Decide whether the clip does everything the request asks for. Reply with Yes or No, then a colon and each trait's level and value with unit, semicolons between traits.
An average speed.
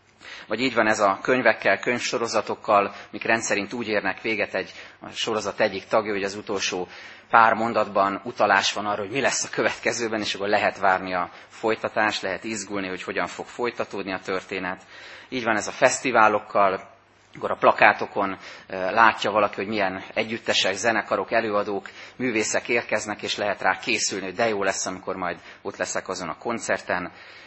No: fast, 165 wpm